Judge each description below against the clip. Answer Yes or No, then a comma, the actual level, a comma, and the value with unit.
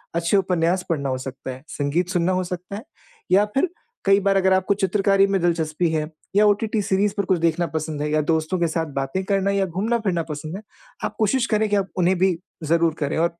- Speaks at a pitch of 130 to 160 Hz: No, medium, 180 Hz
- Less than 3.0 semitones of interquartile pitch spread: No, average, 3.5 semitones